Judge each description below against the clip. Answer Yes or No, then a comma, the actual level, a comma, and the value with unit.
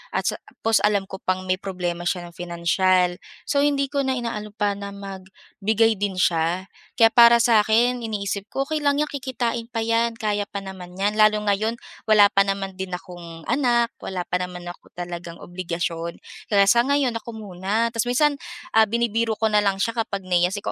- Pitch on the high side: Yes, high, 205 Hz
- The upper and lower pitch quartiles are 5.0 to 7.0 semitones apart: No, average, 3.8 semitones